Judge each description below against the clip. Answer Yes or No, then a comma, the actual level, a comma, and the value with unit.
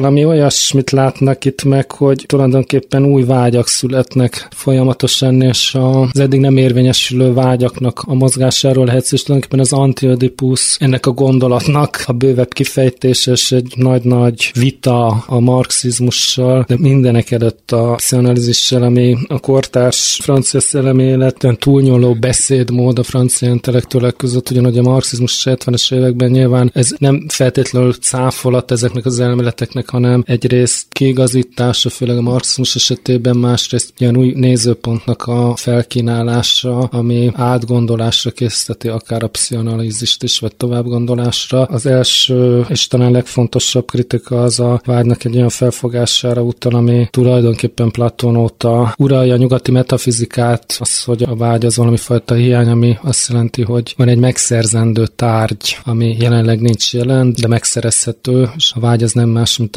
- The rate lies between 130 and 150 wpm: Yes, average, 135 wpm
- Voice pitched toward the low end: Yes, low, 125 Hz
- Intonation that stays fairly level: Yes, narrow, 1.3 semitones